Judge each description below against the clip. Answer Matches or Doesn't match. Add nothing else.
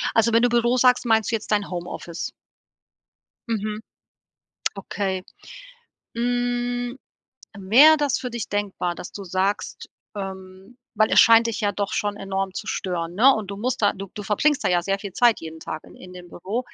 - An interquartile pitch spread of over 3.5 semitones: Matches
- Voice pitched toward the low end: Doesn't match